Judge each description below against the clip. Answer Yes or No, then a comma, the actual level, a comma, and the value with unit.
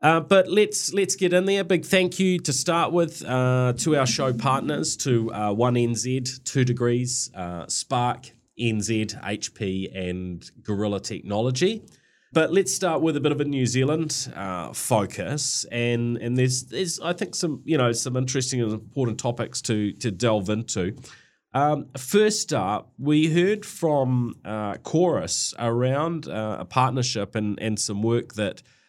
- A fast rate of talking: No, average, 160 wpm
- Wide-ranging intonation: Yes, wide, 6.1 semitones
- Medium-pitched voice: No, low, 125 Hz